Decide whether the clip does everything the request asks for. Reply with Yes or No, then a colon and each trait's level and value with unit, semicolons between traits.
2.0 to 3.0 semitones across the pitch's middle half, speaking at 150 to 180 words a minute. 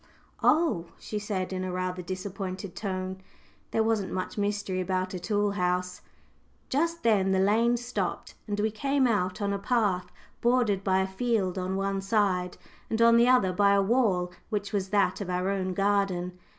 Yes: average, 2.7 semitones; average, 175 wpm